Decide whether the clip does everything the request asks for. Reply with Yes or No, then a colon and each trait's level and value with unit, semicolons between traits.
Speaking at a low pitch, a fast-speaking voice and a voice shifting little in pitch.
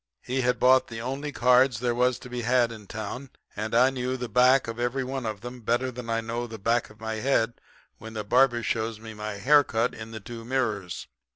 Yes: low, 120 Hz; fast, 225 wpm; narrow, 2.3 semitones